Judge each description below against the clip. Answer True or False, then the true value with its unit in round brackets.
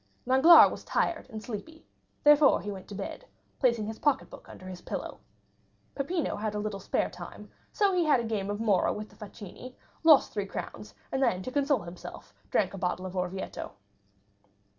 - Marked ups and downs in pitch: True (6.3 semitones)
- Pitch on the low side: False (215 Hz)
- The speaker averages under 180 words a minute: False (185 wpm)